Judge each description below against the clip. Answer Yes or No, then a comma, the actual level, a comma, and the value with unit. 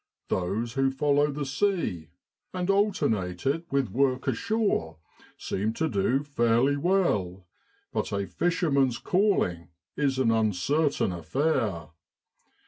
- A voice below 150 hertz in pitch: Yes, low, 135 Hz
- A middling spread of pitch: No, wide, 8.0 semitones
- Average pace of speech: No, slow, 115 wpm